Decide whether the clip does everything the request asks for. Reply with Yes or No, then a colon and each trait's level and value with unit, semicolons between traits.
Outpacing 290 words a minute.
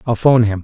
No: fast, 285 wpm